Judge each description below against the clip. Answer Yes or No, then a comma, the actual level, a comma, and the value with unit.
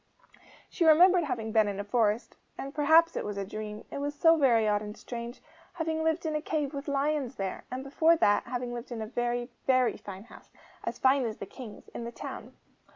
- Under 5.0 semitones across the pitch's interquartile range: No, wide, 5.6 semitones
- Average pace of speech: No, fast, 220 wpm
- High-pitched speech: Yes, very high, 250 Hz